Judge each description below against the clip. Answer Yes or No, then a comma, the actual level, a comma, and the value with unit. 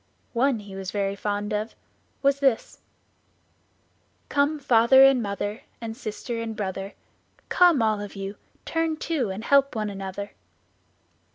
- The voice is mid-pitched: No, high, 220 Hz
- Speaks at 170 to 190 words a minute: No, average, 140 wpm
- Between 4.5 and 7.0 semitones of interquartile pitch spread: Yes, average, 5.0 semitones